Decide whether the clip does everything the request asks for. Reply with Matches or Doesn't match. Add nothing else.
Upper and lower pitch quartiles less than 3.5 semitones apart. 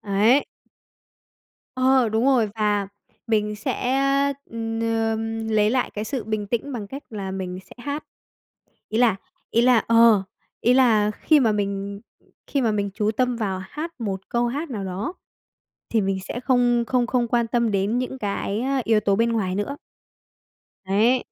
Matches